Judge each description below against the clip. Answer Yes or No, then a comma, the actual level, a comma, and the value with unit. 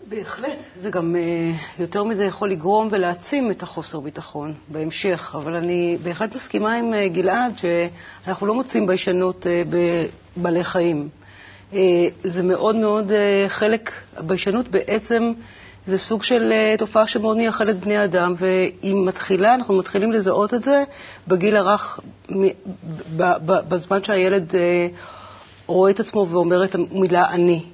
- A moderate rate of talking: Yes, average, 120 wpm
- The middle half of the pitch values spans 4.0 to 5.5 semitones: No, average, 3.3 semitones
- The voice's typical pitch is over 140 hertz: Yes, high, 190 Hz